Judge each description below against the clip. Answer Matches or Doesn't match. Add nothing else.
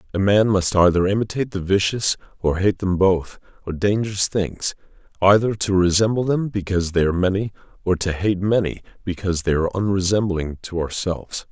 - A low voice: Matches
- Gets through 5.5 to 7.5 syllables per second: Matches